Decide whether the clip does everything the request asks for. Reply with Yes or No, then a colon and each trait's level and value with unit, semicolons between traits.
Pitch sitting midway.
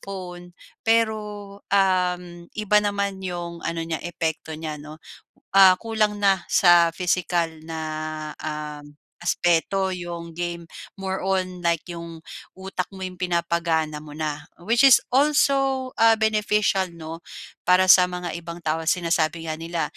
Yes: medium, 175 Hz